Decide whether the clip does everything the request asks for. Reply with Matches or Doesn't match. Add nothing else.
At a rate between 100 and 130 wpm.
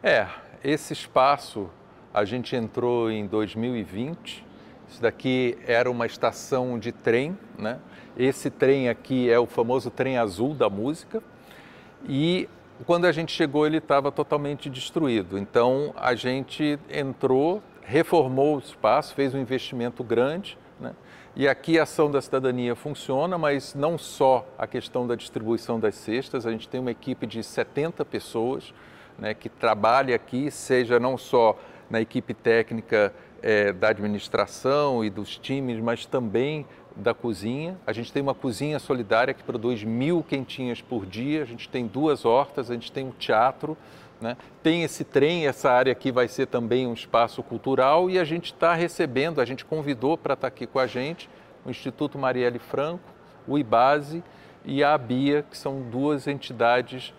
Doesn't match